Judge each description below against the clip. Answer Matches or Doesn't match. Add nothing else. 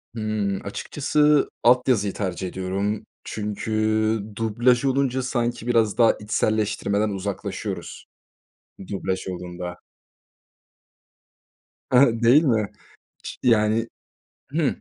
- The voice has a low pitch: Matches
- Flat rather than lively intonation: Doesn't match